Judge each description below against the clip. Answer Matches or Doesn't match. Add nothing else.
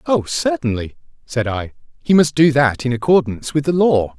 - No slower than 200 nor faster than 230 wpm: Doesn't match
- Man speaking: Matches